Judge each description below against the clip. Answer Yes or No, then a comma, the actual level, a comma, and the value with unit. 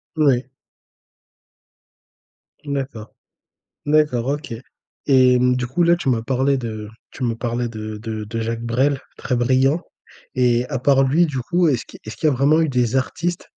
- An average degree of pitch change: Yes, average, 3.3 semitones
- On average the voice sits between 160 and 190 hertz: No, low, 130 Hz